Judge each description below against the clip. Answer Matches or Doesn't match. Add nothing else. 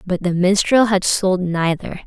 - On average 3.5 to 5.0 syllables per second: Matches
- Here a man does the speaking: Doesn't match